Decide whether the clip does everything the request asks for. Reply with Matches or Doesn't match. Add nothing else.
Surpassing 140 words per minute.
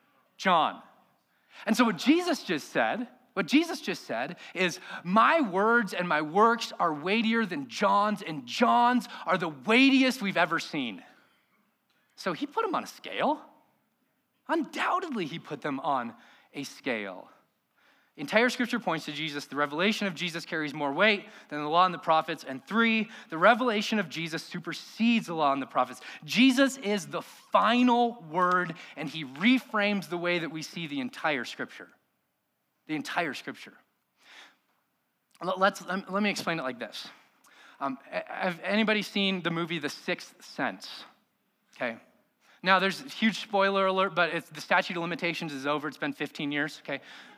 Matches